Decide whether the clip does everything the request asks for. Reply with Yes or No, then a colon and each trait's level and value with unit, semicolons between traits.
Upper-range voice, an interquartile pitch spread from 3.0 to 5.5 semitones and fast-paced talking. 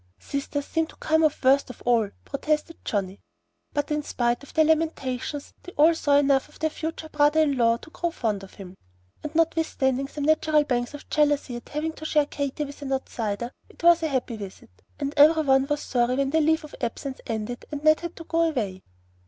Yes: very high, 285 Hz; average, 3.9 semitones; fast, 210 wpm